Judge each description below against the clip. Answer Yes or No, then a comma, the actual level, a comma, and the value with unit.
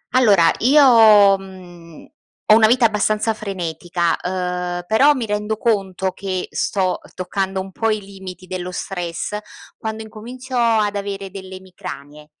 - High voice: Yes, high, 195 Hz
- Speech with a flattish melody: No, average, 3.1 semitones